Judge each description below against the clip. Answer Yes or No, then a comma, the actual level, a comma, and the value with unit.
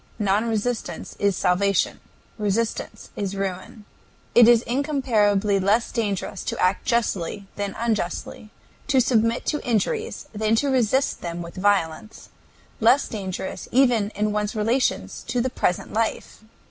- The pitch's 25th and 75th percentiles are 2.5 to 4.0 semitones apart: Yes, average, 3.2 semitones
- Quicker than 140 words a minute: No, slow, 135 wpm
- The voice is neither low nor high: No, high, 215 Hz